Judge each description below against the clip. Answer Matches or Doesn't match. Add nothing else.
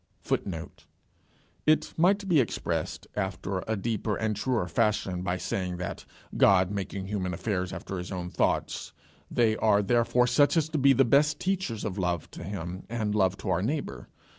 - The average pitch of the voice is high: Doesn't match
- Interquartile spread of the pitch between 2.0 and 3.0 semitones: Doesn't match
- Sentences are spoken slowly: Doesn't match